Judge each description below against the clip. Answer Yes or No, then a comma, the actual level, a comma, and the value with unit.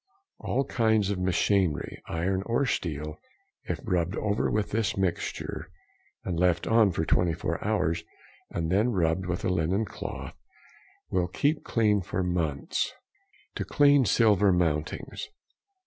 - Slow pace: Yes, slow, 130 wpm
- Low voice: Yes, very low, 95 Hz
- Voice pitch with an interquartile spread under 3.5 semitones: No, average, 4.1 semitones